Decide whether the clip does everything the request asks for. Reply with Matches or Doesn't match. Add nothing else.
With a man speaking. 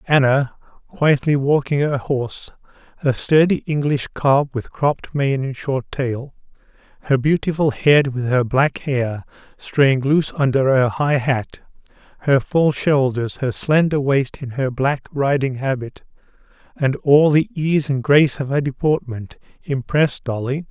Matches